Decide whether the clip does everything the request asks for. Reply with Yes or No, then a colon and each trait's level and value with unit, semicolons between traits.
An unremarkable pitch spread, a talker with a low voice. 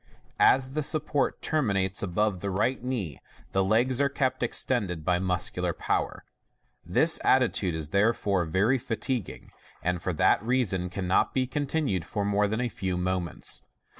No: wide, 5.9 semitones; low, 100 Hz